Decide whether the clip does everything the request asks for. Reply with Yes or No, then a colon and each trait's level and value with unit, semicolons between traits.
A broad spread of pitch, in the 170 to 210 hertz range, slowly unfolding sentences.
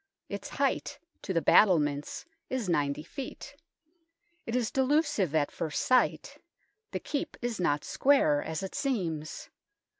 Yes: wide, 8.9 semitones; medium, 185 Hz; slow, 130 wpm